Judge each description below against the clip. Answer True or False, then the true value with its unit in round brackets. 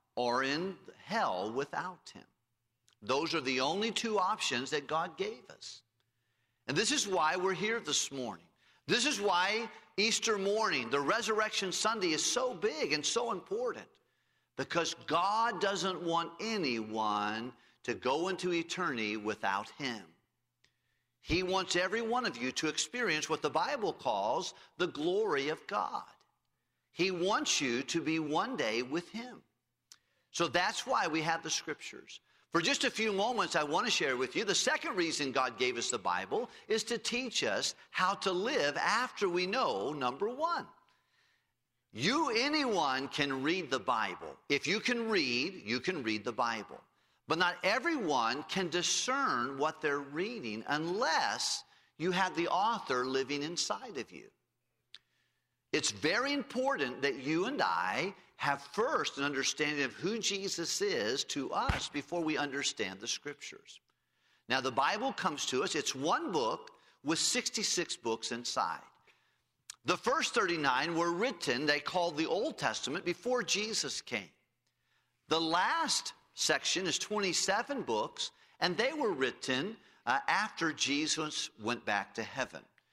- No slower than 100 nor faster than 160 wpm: True (150 wpm)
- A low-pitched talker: False (170 Hz)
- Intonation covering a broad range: True (8.1 semitones)